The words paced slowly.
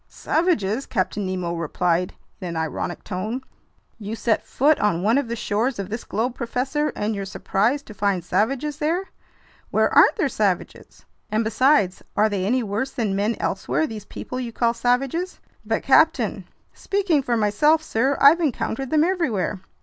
No: average, 165 wpm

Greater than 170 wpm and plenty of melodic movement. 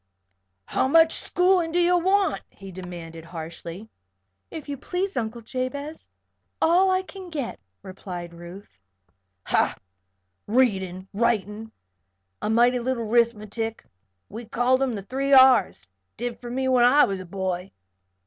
No: average, 140 wpm; wide, 6.4 semitones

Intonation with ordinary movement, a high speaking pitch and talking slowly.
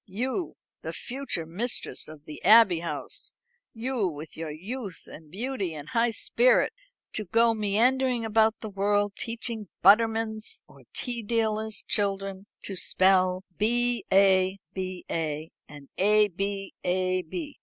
Yes: average, 3.7 semitones; high, 205 Hz; slow, 130 wpm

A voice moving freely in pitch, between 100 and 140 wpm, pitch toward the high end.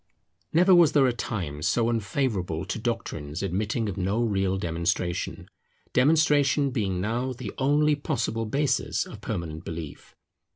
No: wide, 6.6 semitones; slow, 135 wpm; low, 110 Hz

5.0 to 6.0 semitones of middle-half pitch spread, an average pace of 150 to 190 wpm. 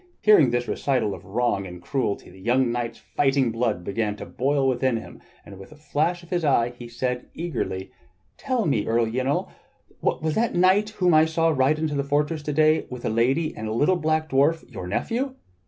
No: average, 5.3 semitones; fast, 205 wpm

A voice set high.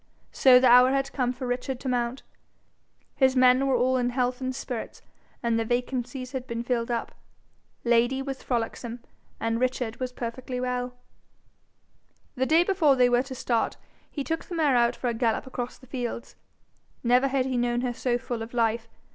Yes: very high, 250 Hz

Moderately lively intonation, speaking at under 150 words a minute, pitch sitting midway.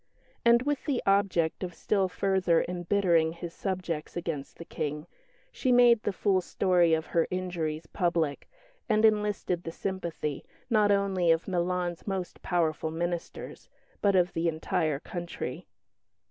Yes: average, 3.1 semitones; average, 140 wpm; medium, 175 Hz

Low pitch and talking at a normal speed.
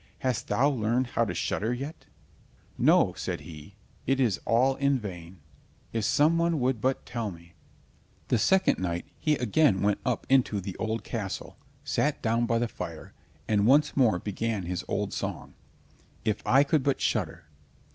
Yes: low, 115 Hz; average, 165 wpm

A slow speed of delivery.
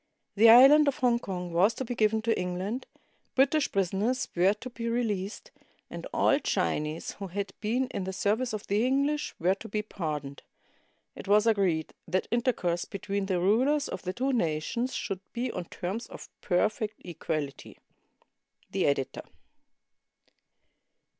No: average, 155 wpm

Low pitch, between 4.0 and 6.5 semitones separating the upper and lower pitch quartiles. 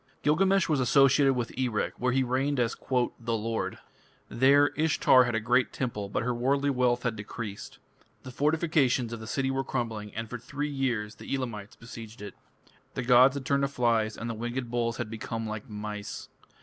No: low, 120 Hz; average, 3.0 semitones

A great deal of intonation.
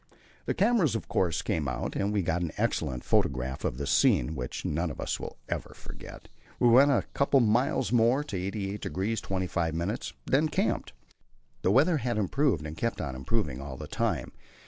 Yes: wide, 7.9 semitones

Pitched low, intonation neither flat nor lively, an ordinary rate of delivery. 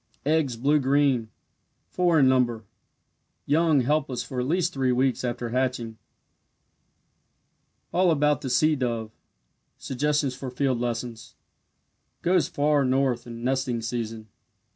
No: low, 130 Hz; average, 3.4 semitones; slow, 120 wpm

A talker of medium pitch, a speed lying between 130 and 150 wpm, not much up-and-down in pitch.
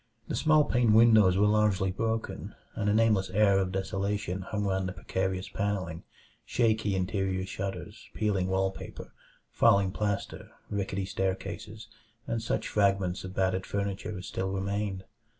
No: low, 100 Hz; average, 145 wpm; narrow, 1.9 semitones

